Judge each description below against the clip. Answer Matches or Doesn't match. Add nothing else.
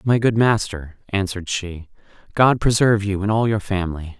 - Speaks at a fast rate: Doesn't match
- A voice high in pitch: Doesn't match